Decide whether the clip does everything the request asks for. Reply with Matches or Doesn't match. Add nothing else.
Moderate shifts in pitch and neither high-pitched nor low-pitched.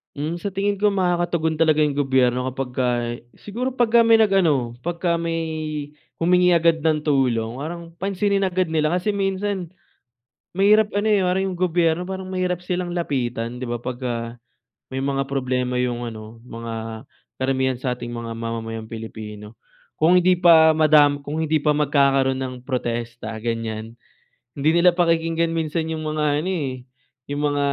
Doesn't match